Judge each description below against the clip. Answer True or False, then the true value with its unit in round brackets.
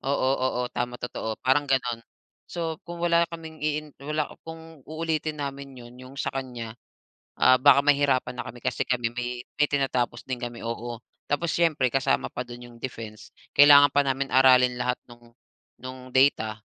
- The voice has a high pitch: False (130 Hz)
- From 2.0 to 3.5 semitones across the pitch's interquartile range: True (3.1 semitones)